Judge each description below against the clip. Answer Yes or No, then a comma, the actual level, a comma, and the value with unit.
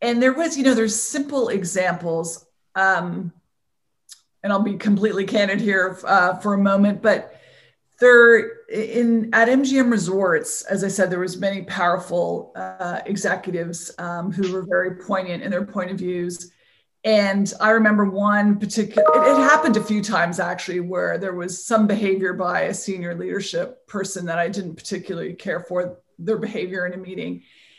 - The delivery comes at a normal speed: Yes, average, 165 wpm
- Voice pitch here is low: No, high, 195 Hz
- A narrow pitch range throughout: No, average, 3.2 semitones